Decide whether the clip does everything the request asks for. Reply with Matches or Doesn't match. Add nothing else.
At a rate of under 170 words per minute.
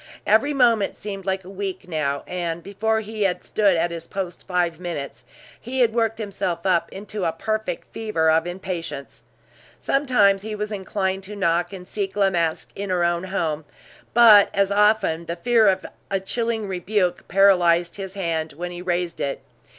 Doesn't match